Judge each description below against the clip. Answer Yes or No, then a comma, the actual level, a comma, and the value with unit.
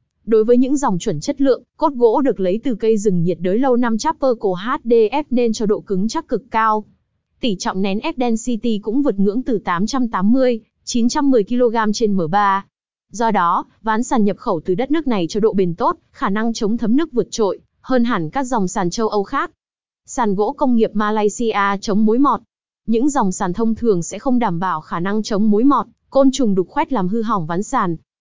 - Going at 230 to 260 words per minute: No, average, 215 wpm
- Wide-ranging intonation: No, average, 3.7 semitones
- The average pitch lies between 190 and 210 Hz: No, high, 225 Hz